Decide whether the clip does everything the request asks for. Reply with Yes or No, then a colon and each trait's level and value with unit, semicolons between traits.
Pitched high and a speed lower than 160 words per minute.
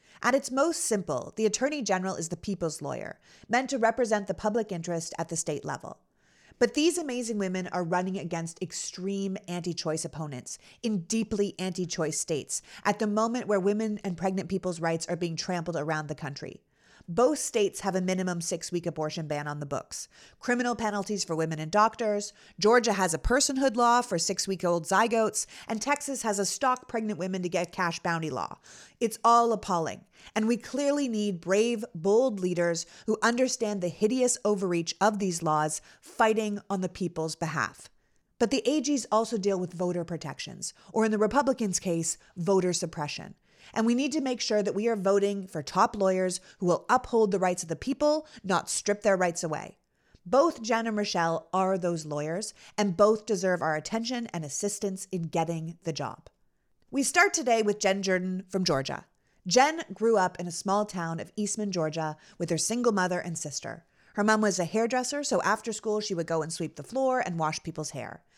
No: high, 195 Hz; average, 190 wpm